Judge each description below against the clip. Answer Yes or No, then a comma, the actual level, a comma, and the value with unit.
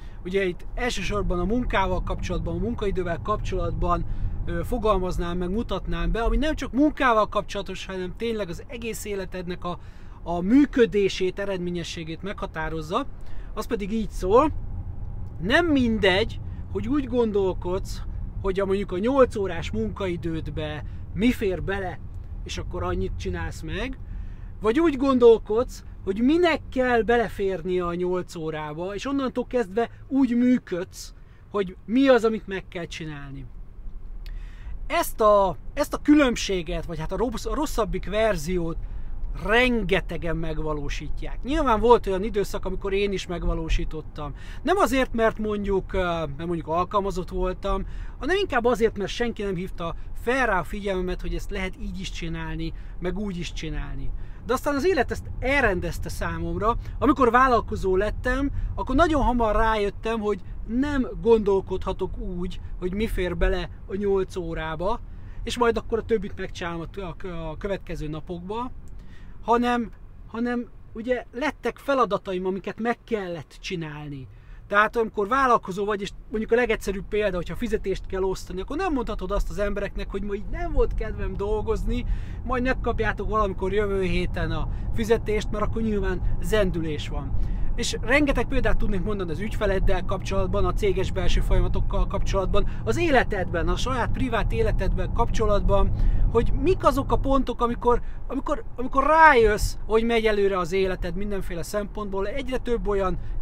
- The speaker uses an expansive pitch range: Yes, wide, 6.0 semitones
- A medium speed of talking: Yes, average, 140 wpm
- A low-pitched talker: No, high, 195 Hz